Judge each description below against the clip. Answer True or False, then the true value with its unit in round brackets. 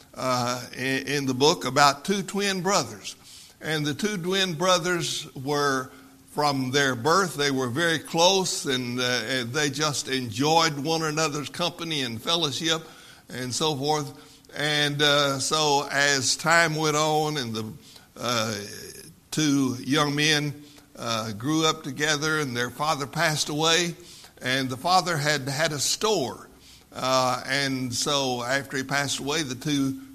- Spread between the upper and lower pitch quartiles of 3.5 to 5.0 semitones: False (3.0 semitones)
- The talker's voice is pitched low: False (145 Hz)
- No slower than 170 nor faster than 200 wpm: False (145 wpm)